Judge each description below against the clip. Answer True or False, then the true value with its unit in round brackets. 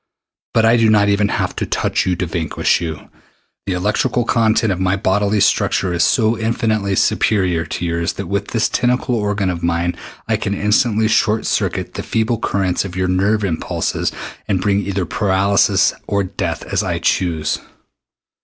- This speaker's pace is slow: False (175 wpm)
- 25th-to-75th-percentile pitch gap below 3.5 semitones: True (3.1 semitones)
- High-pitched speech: False (100 Hz)